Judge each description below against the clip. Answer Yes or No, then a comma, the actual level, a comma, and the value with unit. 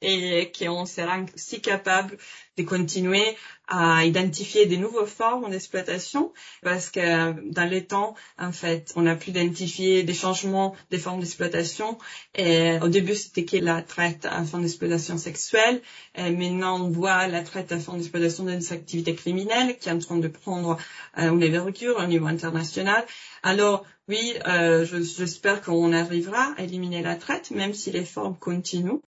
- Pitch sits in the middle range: Yes, medium, 180 Hz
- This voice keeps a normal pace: Yes, average, 160 wpm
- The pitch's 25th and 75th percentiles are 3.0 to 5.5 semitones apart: No, narrow, 2.4 semitones